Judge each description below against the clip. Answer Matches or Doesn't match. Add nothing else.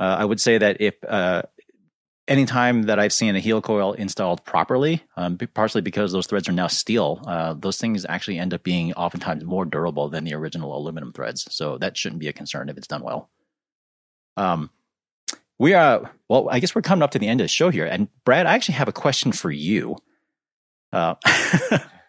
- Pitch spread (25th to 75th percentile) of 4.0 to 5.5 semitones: Matches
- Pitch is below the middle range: Matches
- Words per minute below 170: Doesn't match